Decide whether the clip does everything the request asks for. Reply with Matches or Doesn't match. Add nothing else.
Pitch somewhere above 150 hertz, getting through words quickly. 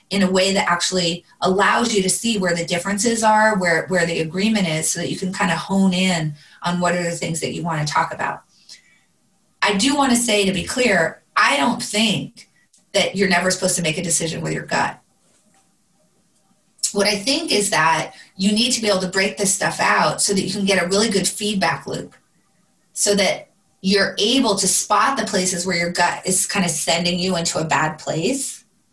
Matches